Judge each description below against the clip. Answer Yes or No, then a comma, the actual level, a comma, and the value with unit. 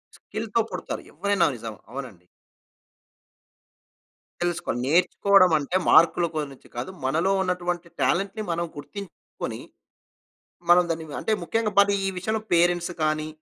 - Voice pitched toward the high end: No, medium, 175 Hz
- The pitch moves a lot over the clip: No, average, 4.3 semitones